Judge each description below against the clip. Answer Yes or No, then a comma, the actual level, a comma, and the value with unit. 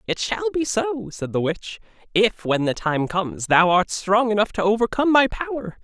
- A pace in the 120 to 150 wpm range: No, fast, 205 wpm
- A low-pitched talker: No, high, 195 Hz